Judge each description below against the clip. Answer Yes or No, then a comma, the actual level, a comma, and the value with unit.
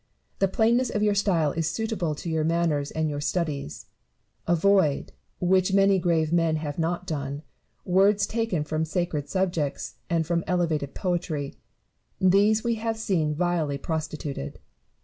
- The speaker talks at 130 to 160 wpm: Yes, average, 145 wpm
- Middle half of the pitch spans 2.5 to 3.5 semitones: No, average, 3.9 semitones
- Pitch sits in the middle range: Yes, medium, 170 Hz